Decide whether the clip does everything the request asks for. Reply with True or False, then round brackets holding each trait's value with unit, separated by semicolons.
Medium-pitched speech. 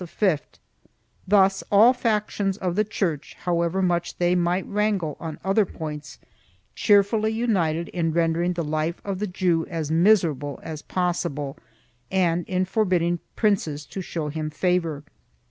True (175 Hz)